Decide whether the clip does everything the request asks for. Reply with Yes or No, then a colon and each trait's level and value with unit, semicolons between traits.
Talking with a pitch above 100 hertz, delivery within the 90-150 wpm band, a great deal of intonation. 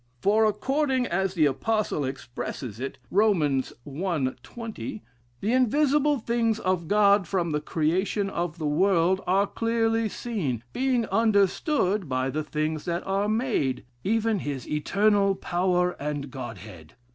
Yes: high, 190 Hz; slow, 135 wpm; wide, 6.7 semitones